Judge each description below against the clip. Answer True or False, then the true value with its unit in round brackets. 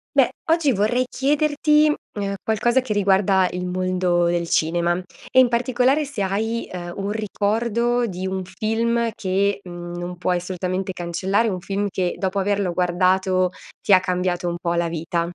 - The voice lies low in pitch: False (190 Hz)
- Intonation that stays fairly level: False (4.1 semitones)